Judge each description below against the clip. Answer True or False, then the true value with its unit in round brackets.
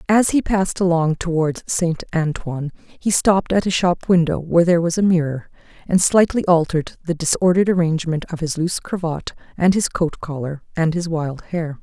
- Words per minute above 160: True (185 wpm)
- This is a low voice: False (170 Hz)